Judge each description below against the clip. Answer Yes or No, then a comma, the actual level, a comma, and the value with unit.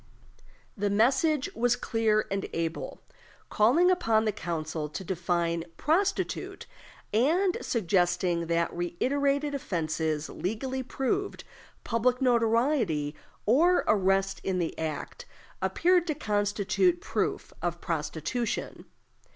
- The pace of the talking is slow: Yes, slow, 100 wpm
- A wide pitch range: Yes, wide, 7.7 semitones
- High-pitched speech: Yes, high, 215 Hz